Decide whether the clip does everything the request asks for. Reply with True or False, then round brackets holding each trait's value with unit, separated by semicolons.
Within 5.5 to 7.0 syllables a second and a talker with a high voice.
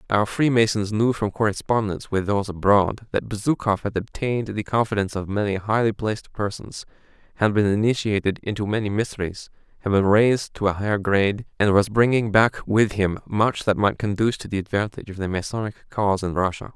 False (6.0 syllables/s; 105 Hz)